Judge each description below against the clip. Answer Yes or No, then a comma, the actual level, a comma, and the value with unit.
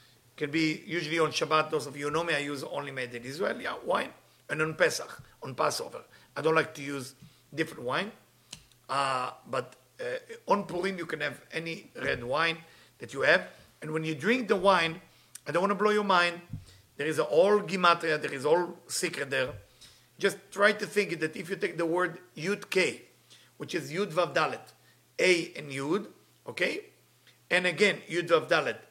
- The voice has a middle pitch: Yes, medium, 165 Hz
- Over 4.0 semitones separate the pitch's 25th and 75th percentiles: Yes, average, 4.5 semitones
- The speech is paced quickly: No, average, 190 wpm